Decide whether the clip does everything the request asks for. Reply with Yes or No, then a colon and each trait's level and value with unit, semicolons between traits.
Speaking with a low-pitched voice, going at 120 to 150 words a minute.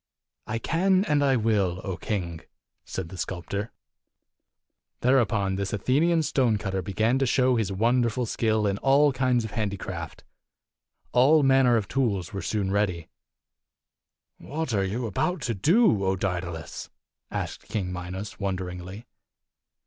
Yes: low, 110 Hz; slow, 135 wpm